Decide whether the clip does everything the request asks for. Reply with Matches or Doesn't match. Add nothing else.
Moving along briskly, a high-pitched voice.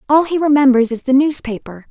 Doesn't match